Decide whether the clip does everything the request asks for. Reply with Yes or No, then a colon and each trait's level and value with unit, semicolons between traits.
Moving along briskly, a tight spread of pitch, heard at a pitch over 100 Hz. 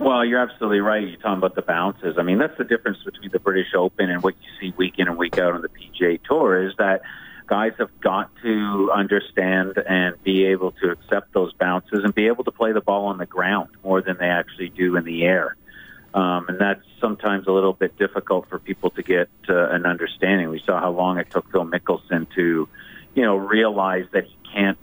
No: fast, 225 wpm; narrow, 1.9 semitones; very low, 95 Hz